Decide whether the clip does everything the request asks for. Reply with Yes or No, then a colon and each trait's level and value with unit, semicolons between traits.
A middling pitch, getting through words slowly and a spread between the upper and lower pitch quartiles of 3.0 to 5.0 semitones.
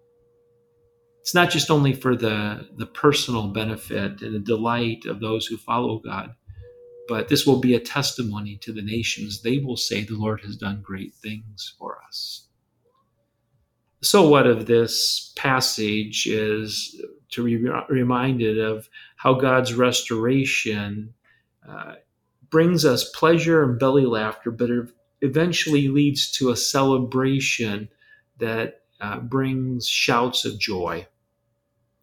No: low, 120 Hz; slow, 130 wpm; average, 4.0 semitones